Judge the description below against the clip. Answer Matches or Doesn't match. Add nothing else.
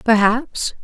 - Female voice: Matches